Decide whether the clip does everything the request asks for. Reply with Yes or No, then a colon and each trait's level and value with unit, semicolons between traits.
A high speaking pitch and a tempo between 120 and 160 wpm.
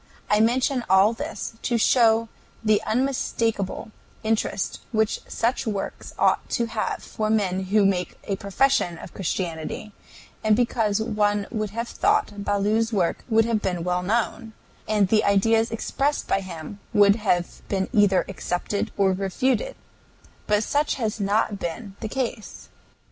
Yes: high, 215 Hz; average, 145 wpm